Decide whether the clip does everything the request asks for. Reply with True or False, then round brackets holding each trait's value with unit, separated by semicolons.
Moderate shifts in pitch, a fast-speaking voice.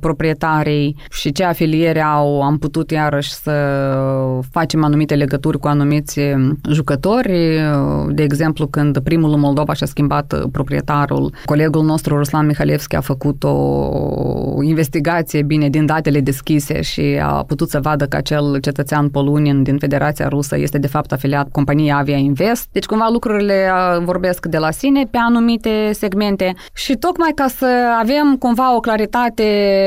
False (4.3 semitones; 145 wpm)